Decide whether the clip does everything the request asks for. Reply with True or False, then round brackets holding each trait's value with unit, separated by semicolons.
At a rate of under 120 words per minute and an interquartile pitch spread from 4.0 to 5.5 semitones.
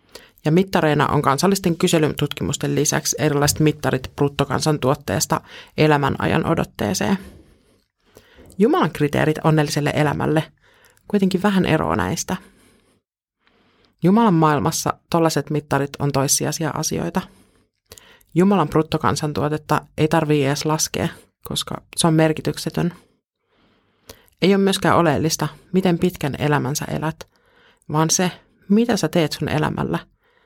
False (100 wpm; 3.2 semitones)